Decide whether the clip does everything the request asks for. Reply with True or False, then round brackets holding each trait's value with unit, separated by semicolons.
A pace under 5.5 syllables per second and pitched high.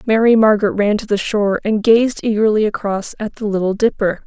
False (5.6 syllables/s; 215 Hz)